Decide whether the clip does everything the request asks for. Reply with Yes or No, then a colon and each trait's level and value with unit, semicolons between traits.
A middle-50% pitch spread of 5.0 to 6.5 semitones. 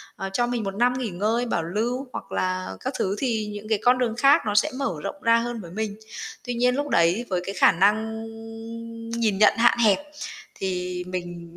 No: average, 4.5 semitones